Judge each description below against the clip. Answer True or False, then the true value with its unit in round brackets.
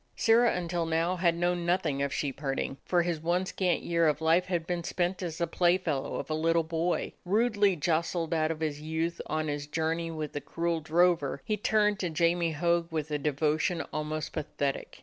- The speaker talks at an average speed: True (195 wpm)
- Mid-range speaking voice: True (165 Hz)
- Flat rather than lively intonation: True (2.1 semitones)